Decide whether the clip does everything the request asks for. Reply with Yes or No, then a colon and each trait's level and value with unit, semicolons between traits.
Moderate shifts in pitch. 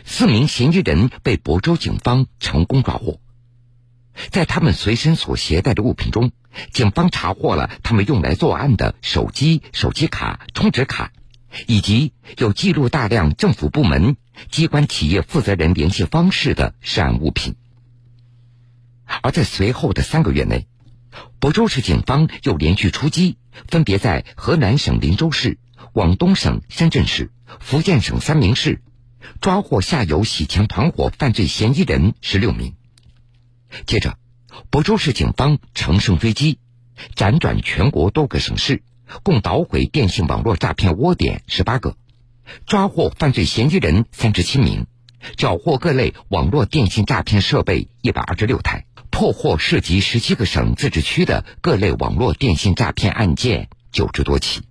Yes: average, 4.8 semitones